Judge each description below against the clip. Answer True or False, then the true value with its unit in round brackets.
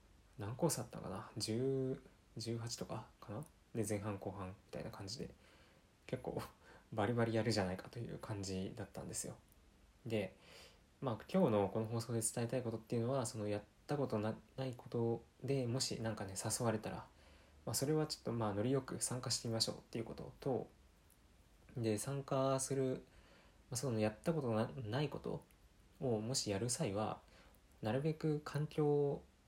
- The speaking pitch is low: True (115 Hz)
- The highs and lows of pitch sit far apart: False (4.2 semitones)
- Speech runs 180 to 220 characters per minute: False (320 characters per minute)